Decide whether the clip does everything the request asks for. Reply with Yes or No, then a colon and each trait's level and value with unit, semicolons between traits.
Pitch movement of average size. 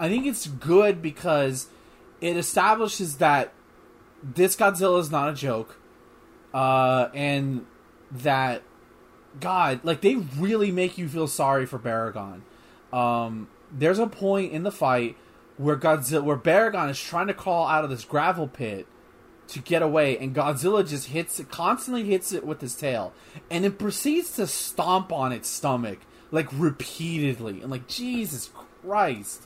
No: wide, 5.9 semitones